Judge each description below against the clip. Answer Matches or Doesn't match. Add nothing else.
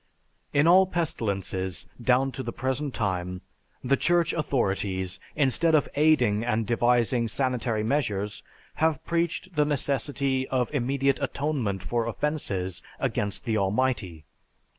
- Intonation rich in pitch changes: Matches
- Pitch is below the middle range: Matches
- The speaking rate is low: Matches